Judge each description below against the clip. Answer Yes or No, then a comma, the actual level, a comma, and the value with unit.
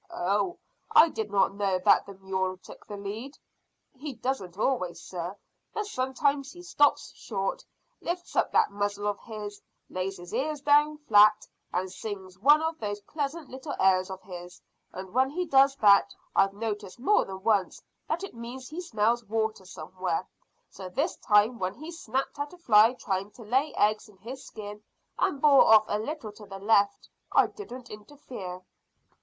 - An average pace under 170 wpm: No, average, 175 wpm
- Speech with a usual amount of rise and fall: No, wide, 5.9 semitones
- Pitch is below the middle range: No, high, 215 Hz